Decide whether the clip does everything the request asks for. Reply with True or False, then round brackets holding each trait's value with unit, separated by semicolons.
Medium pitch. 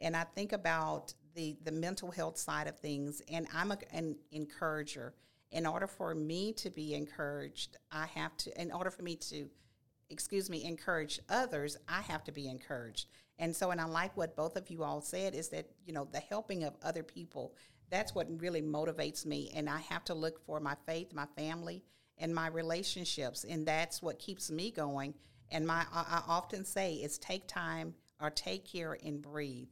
True (160 Hz)